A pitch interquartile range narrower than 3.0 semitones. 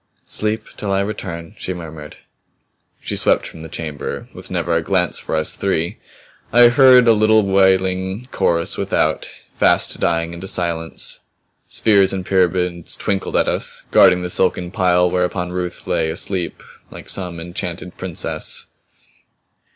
Yes: narrow, 2.4 semitones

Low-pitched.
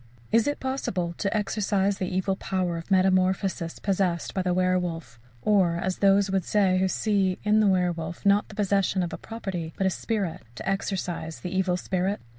No: high, 190 Hz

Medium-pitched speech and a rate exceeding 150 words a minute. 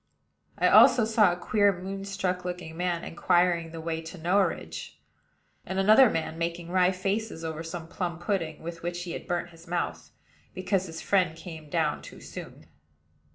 Yes: medium, 175 Hz; average, 165 wpm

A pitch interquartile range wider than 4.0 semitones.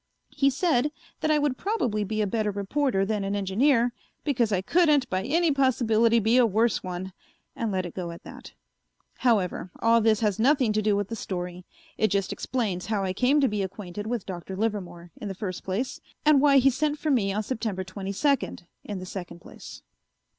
Yes: average, 5.0 semitones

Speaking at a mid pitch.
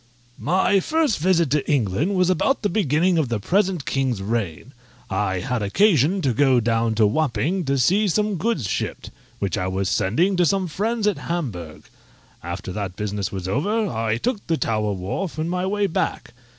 Yes: medium, 145 Hz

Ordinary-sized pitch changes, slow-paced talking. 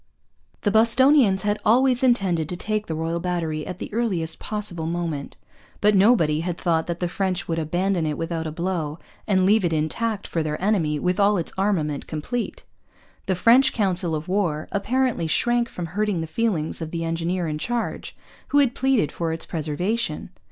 No: average, 4.7 semitones; average, 180 wpm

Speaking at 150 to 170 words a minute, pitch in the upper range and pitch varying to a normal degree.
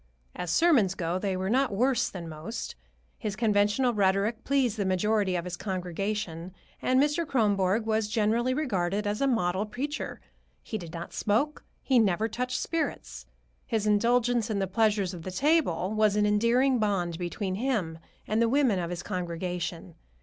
Yes: average, 165 wpm; high, 210 Hz; average, 4.4 semitones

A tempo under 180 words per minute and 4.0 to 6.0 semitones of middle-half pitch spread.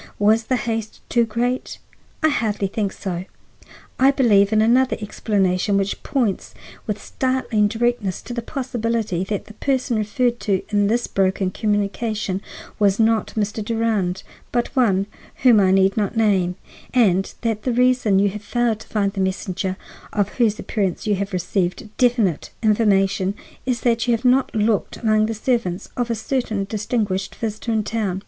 No: average, 165 wpm; average, 3.0 semitones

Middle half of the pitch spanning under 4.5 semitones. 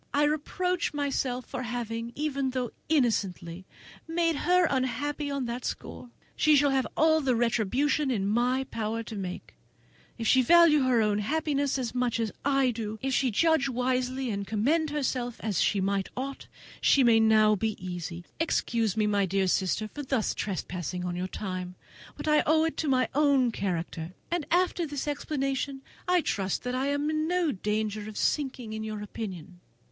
No: average, 5.1 semitones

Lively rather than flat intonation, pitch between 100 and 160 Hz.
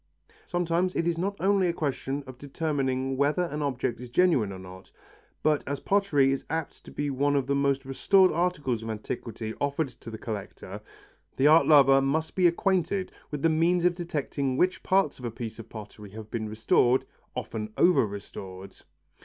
Yes: wide, 5.8 semitones; medium, 140 Hz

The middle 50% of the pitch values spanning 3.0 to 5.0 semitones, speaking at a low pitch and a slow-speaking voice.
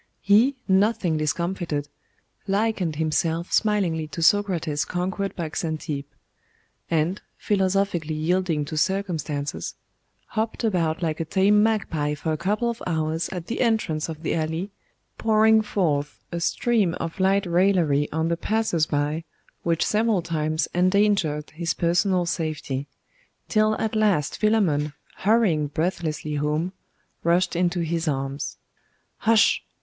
No: average, 4.3 semitones; medium, 170 Hz; slow, 125 wpm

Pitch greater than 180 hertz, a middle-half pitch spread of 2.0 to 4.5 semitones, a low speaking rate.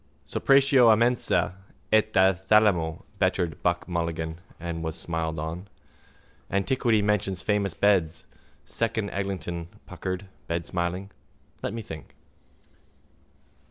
No: very low, 95 Hz; average, 3.8 semitones; slow, 105 wpm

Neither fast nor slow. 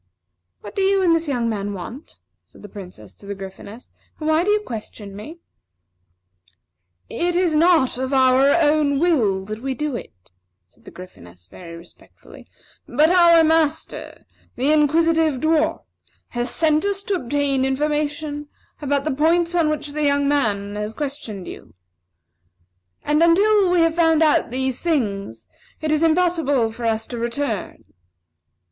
Yes: average, 155 wpm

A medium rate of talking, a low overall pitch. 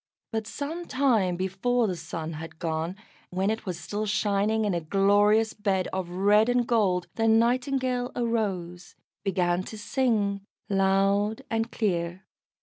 No: average, 145 wpm; high, 205 Hz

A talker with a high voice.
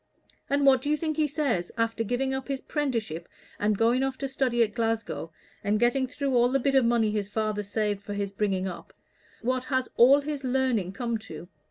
Yes: high, 240 Hz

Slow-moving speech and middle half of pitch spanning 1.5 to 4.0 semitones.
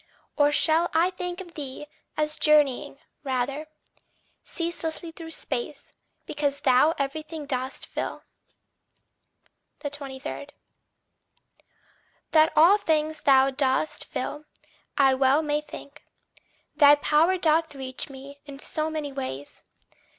Yes: slow, 110 wpm; narrow, 2.6 semitones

